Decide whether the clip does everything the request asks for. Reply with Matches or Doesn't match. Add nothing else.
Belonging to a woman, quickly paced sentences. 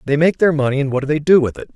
Doesn't match